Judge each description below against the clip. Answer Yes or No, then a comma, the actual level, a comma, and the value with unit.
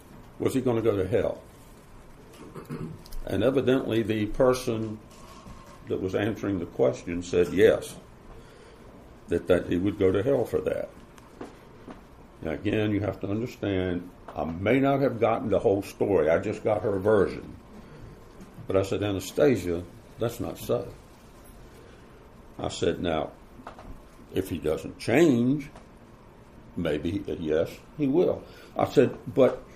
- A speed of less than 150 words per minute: Yes, slow, 135 wpm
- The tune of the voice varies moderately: Yes, average, 5.0 semitones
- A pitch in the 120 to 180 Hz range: No, low, 110 Hz